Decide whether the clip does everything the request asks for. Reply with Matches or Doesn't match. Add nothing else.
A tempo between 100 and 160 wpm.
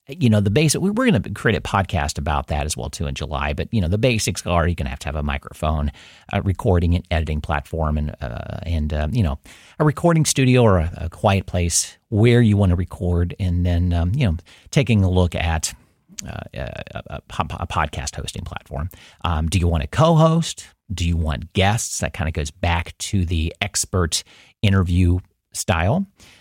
Doesn't match